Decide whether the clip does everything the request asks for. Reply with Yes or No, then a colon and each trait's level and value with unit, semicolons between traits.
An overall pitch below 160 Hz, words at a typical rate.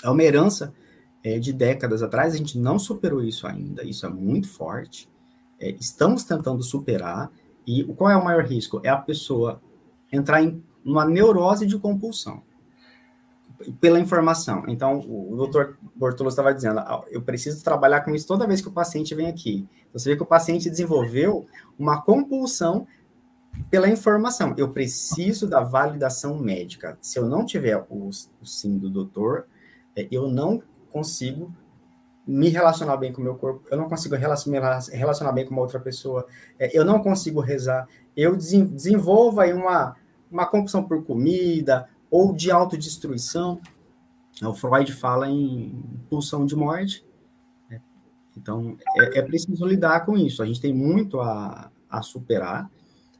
Yes: medium, 140 Hz; average, 155 wpm